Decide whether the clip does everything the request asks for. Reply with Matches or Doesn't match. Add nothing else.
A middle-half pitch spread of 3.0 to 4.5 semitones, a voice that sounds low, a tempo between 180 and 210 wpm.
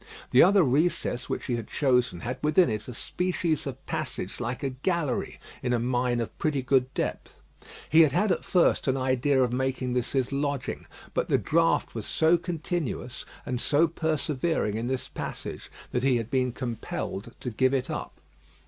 Matches